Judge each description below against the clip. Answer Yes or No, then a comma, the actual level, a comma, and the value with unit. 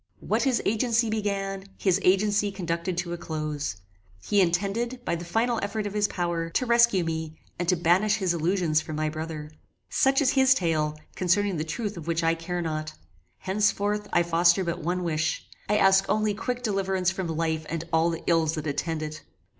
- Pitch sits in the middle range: Yes, medium, 180 Hz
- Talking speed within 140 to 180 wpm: No, average, 190 wpm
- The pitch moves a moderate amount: Yes, average, 4.0 semitones